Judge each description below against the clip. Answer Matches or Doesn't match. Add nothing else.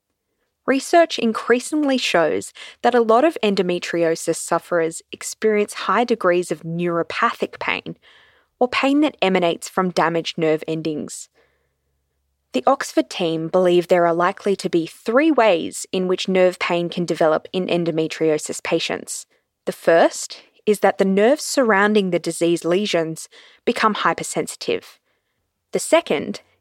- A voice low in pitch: Doesn't match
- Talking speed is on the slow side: Matches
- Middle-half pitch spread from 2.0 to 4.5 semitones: Doesn't match